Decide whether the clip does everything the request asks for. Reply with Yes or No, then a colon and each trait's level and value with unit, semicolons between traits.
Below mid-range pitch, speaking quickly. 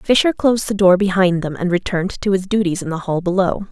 No: high, 190 Hz; fast, 240 wpm